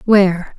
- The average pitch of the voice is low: No, high, 190 Hz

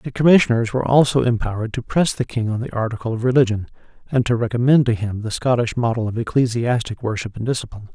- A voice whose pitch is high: No, low, 120 Hz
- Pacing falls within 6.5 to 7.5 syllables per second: Yes, 6.7 syllables/s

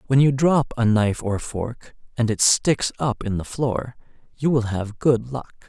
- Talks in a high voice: No, low, 120 Hz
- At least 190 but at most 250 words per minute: Yes, average, 200 wpm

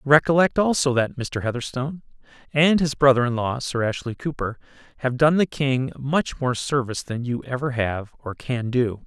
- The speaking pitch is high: No, low, 130 Hz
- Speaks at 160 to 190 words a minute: Yes, average, 180 wpm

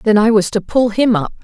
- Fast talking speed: Yes, fast, 295 wpm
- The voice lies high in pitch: Yes, high, 215 Hz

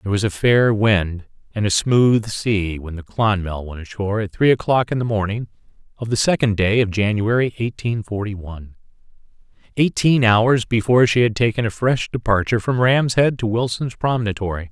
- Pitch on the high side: No, low, 110 Hz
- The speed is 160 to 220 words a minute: Yes, average, 180 wpm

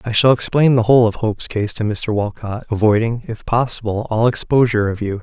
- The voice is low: Yes, low, 110 Hz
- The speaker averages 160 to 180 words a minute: No, fast, 205 wpm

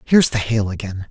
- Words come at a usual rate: No, fast, 215 wpm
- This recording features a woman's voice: No, male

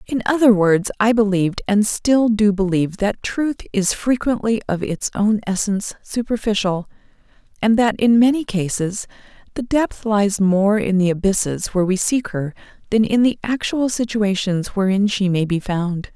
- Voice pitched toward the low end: No, high, 210 Hz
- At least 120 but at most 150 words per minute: No, average, 165 wpm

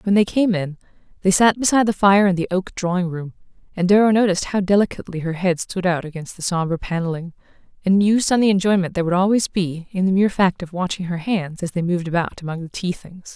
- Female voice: Yes, female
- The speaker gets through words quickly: Yes, fast, 235 wpm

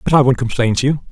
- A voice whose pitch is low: Yes, low, 130 Hz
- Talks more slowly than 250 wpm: No, fast, 320 wpm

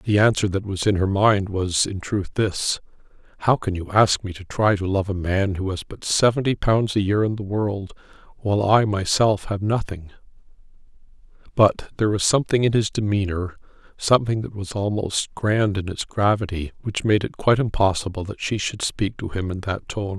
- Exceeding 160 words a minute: Yes, average, 190 wpm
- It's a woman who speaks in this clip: No, male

